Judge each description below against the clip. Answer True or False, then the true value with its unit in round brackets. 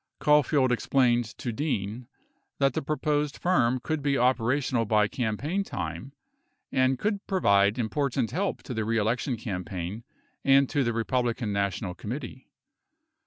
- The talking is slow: True (130 wpm)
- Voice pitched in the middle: False (125 Hz)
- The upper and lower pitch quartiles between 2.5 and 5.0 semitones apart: True (4.2 semitones)